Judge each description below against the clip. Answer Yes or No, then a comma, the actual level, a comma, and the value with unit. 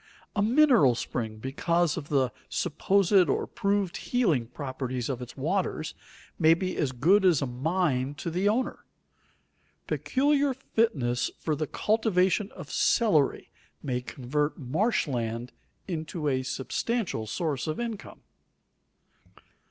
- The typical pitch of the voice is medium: Yes, medium, 160 Hz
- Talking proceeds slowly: Yes, slow, 125 wpm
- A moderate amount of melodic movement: No, wide, 7.3 semitones